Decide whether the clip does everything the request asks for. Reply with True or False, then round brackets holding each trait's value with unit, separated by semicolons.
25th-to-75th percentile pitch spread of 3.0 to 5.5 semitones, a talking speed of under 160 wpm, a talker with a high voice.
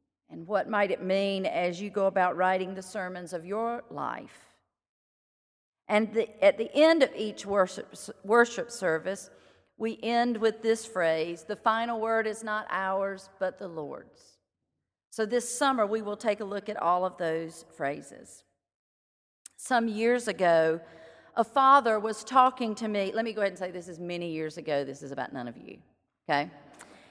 False (4.7 semitones; 175 wpm; 200 Hz)